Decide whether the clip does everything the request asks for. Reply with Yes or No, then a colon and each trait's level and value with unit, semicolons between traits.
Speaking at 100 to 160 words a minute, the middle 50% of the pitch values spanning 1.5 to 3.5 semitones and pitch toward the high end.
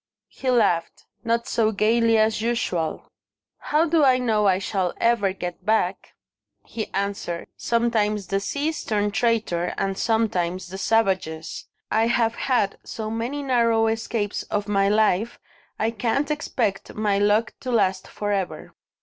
Yes: average, 145 wpm; average, 3.0 semitones; high, 215 Hz